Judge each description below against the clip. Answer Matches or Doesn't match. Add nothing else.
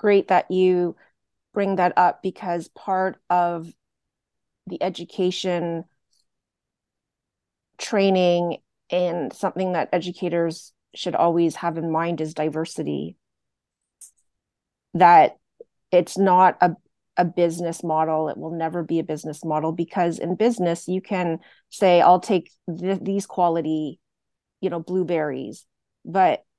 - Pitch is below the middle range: Doesn't match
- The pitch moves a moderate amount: Doesn't match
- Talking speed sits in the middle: Doesn't match